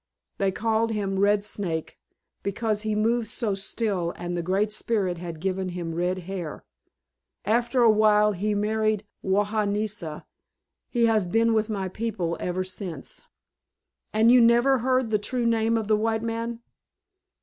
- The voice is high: Yes, high, 210 Hz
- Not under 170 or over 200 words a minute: No, average, 150 wpm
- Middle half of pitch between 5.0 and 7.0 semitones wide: No, average, 3.1 semitones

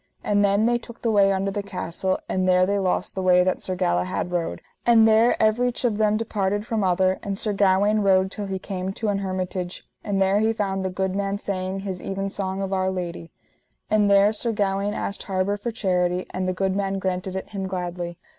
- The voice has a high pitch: Yes, high, 195 Hz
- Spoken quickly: Yes, fast, 215 wpm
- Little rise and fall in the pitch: Yes, narrow, 1.7 semitones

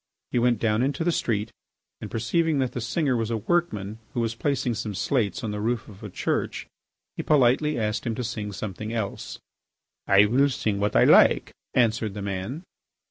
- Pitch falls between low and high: No, low, 115 Hz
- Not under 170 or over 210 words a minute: Yes, average, 190 wpm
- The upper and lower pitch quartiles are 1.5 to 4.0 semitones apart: Yes, average, 3.4 semitones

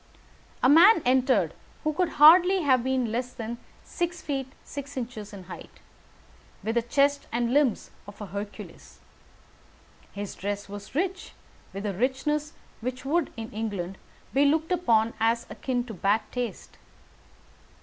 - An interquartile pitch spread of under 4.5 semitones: No, average, 5.0 semitones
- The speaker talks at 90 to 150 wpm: Yes, average, 145 wpm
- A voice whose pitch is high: Yes, very high, 250 Hz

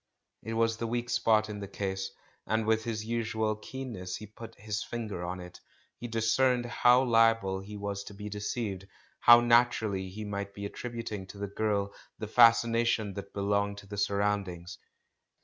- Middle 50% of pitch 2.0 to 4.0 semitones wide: Yes, narrow, 2.4 semitones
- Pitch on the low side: Yes, low, 105 Hz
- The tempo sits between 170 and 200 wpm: Yes, average, 185 wpm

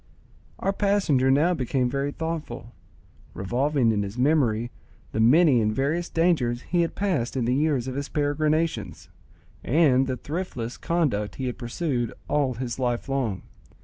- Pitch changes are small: No, average, 4.5 semitones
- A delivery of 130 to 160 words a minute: Yes, average, 150 wpm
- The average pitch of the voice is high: No, low, 135 Hz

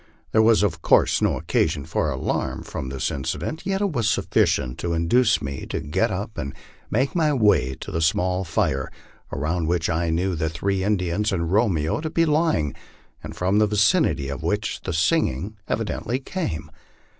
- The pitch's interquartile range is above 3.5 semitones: Yes, wide, 5.6 semitones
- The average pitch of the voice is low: Yes, very low, 90 Hz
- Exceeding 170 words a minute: Yes, average, 180 wpm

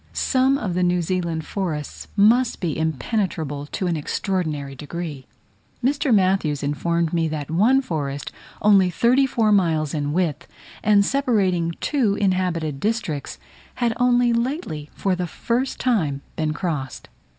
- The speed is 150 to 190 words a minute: No, average, 140 wpm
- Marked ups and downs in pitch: Yes, wide, 6.2 semitones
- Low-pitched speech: No, medium, 180 Hz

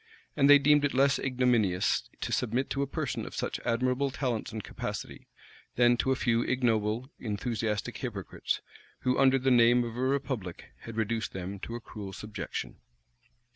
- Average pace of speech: Yes, average, 170 wpm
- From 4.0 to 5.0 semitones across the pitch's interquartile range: No, average, 3.1 semitones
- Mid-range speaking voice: No, low, 120 Hz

